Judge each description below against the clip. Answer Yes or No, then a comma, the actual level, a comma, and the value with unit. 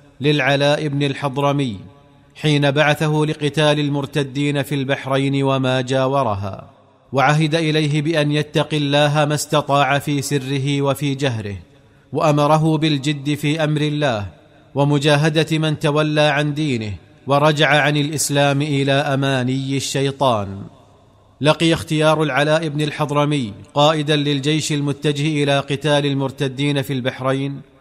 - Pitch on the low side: No, medium, 145 Hz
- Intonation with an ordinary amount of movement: No, narrow, 1.6 semitones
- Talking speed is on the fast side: No, average, 110 wpm